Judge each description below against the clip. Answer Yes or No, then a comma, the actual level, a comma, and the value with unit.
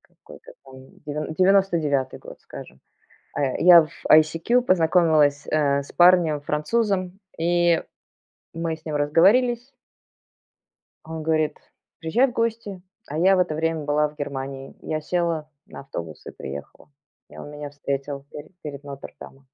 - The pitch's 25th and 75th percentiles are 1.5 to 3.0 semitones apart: No, average, 3.6 semitones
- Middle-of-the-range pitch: Yes, medium, 155 Hz